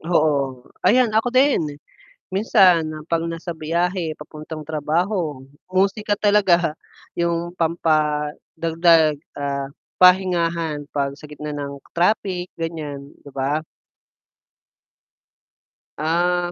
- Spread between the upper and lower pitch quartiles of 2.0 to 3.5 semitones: Yes, average, 3.0 semitones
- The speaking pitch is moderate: Yes, medium, 165 Hz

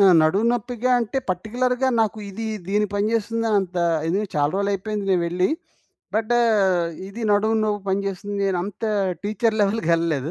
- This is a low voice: No, high, 205 Hz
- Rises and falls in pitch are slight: No, average, 3.0 semitones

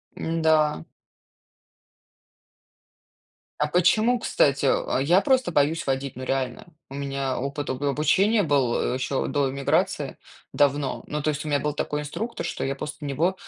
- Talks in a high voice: No, medium, 145 Hz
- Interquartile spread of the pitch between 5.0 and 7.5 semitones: No, average, 2.7 semitones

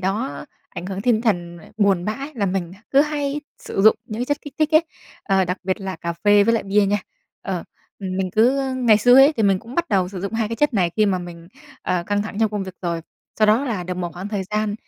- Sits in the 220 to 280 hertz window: No, high, 205 Hz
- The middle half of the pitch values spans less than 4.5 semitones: Yes, average, 3.8 semitones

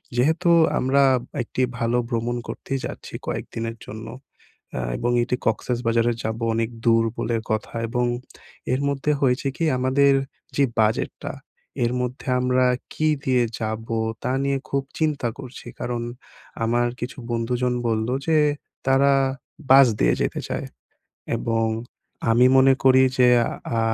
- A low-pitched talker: Yes, low, 125 Hz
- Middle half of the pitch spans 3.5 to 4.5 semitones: No, average, 2.7 semitones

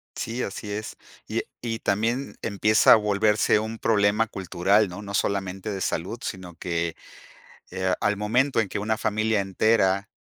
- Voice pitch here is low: Yes, low, 105 Hz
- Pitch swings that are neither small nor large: No, narrow, 2.3 semitones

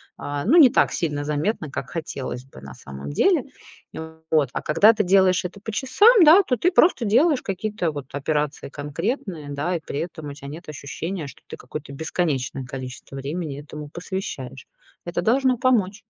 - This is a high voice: No, medium, 160 Hz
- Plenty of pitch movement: Yes, wide, 6.4 semitones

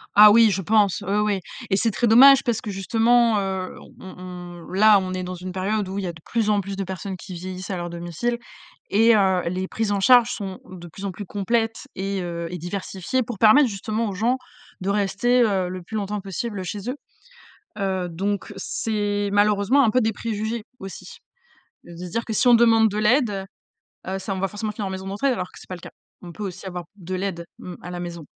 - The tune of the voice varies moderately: Yes, average, 3.0 semitones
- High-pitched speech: Yes, high, 200 Hz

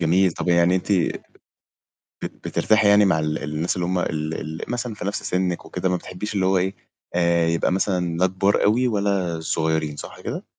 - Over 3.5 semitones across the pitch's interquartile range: No, average, 2.9 semitones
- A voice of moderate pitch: No, very low, 90 Hz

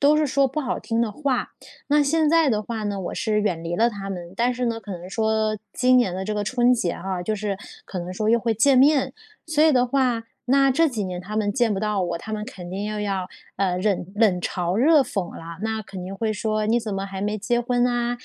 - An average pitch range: Yes, average, 4.2 semitones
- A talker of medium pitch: No, high, 215 Hz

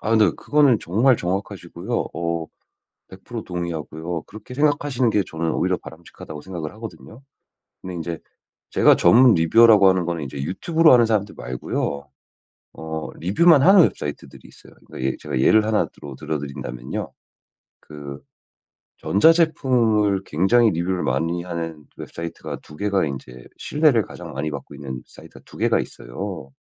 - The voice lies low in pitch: Yes, very low, 90 Hz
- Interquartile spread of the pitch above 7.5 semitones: No, wide, 6.7 semitones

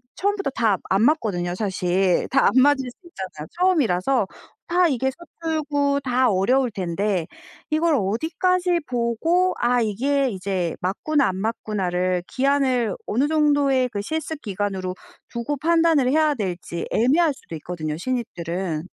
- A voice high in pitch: Yes, high, 245 Hz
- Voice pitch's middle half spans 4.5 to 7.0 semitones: No, wide, 7.4 semitones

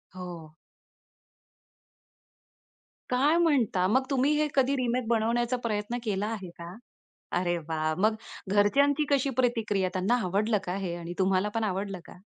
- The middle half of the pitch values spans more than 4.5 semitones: Yes, average, 5.2 semitones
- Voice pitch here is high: Yes, high, 210 Hz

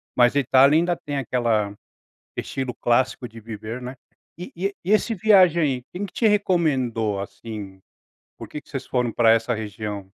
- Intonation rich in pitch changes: Yes, wide, 6.6 semitones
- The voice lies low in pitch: Yes, low, 125 Hz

